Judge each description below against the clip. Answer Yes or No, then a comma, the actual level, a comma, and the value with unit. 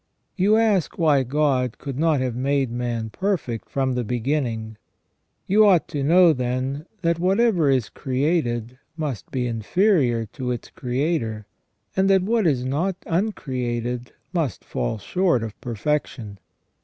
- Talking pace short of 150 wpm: Yes, average, 140 wpm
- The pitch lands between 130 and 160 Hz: Yes, low, 135 Hz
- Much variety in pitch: Yes, wide, 5.8 semitones